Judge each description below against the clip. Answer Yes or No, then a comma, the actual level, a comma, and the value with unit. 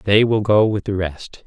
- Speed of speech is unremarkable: No, fast, 245 wpm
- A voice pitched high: No, low, 100 Hz